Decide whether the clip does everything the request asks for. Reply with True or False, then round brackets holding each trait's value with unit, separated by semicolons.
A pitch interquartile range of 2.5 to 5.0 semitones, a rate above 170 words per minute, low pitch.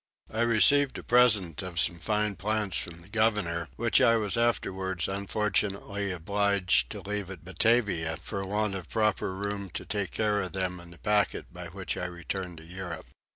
True (2.9 semitones; 180 wpm; 100 Hz)